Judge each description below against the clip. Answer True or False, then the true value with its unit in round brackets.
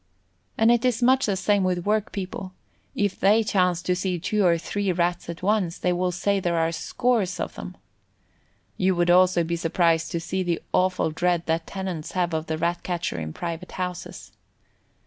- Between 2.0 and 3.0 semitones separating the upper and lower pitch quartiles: True (2.4 semitones)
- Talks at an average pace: True (185 wpm)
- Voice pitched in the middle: True (180 Hz)